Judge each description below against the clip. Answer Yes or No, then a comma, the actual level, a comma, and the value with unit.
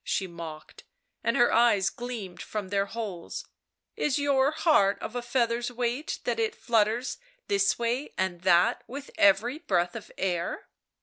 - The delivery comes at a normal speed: Yes, average, 150 wpm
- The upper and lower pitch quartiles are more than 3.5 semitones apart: Yes, average, 4.5 semitones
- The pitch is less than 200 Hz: No, high, 230 Hz